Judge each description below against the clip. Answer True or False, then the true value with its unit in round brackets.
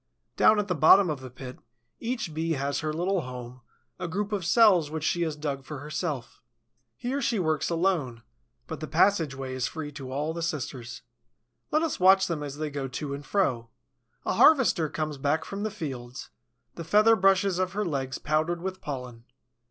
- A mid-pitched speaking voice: True (155 Hz)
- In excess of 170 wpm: True (190 wpm)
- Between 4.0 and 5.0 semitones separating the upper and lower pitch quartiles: False (5.5 semitones)